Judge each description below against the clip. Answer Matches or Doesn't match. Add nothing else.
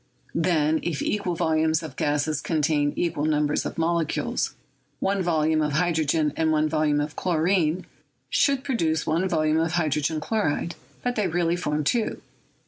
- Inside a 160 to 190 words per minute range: Doesn't match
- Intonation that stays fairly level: Matches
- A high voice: Doesn't match